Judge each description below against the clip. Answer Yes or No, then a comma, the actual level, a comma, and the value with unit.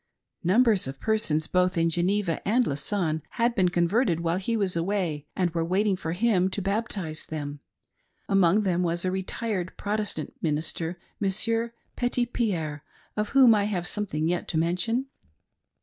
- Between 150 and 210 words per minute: Yes, average, 155 wpm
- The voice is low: No, medium, 185 Hz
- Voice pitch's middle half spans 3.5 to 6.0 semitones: Yes, average, 4.2 semitones